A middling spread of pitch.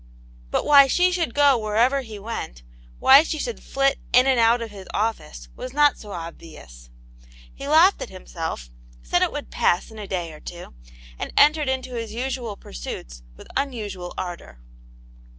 No: wide, 7.6 semitones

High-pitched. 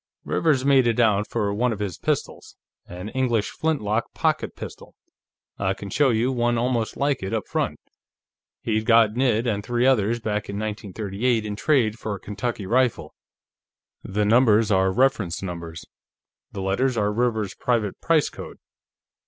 No: low, 110 Hz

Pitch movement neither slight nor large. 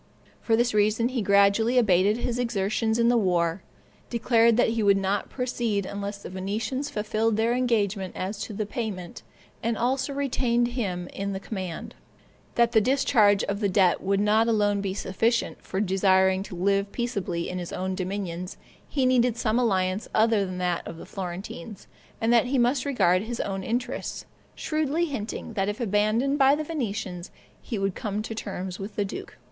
Yes: average, 3.6 semitones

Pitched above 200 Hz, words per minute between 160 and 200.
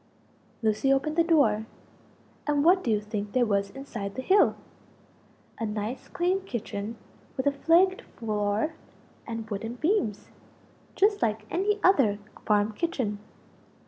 No: high, 235 Hz; slow, 135 wpm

